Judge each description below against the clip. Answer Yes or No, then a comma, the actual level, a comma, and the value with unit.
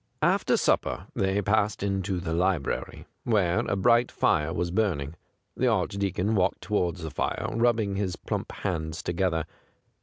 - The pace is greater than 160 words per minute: No, average, 145 wpm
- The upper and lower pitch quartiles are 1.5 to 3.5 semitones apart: Yes, average, 3.1 semitones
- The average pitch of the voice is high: No, very low, 95 Hz